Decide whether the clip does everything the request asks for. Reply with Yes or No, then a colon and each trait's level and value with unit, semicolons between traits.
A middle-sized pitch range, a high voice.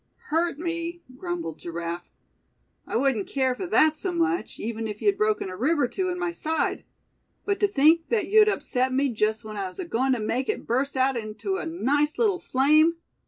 No: wide, 6.7 semitones; very high, 295 Hz